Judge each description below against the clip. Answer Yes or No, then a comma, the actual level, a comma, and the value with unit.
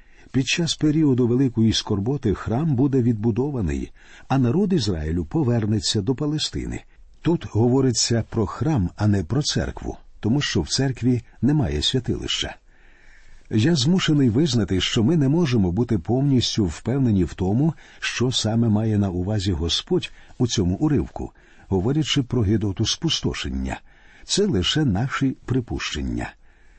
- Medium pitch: No, low, 120 Hz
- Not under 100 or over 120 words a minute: No, average, 130 wpm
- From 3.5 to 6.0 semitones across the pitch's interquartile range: Yes, wide, 5.4 semitones